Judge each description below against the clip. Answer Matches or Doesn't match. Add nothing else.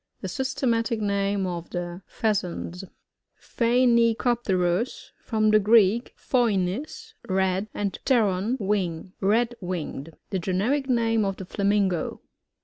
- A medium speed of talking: Doesn't match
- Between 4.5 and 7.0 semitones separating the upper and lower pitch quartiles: Doesn't match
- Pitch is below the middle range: Doesn't match